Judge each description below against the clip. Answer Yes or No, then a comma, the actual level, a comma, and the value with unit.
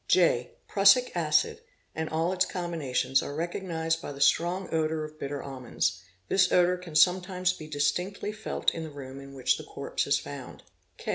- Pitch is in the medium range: Yes, medium, 160 Hz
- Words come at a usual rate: Yes, average, 170 wpm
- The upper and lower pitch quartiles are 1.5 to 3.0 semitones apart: No, average, 4.3 semitones